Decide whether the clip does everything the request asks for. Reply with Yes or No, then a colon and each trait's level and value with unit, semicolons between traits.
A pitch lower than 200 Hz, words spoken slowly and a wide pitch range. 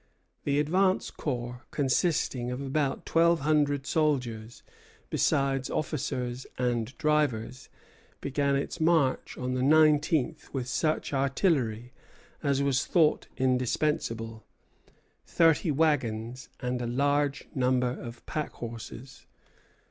No: low, 135 Hz; slow, 100 wpm; average, 3.4 semitones